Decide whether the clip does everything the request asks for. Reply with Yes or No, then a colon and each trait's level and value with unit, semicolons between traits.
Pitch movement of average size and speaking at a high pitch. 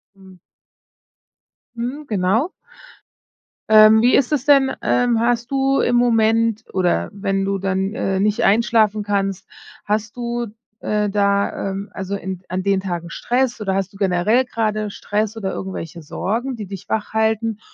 Yes: average, 3.2 semitones; high, 210 Hz